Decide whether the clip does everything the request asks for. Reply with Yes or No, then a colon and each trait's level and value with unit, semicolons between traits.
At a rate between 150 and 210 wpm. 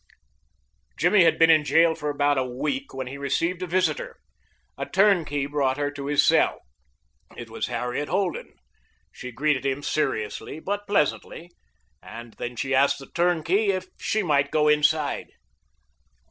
Yes: average, 155 wpm